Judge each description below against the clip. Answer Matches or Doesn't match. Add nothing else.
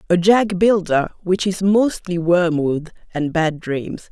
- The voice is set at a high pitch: Doesn't match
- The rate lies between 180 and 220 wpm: Doesn't match